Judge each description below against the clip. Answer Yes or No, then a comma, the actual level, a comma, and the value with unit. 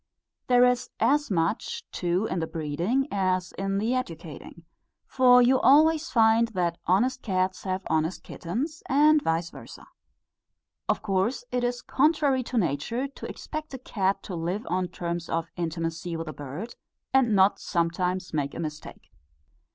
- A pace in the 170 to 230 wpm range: No, average, 155 wpm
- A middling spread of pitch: No, wide, 6.7 semitones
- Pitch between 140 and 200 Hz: Yes, high, 190 Hz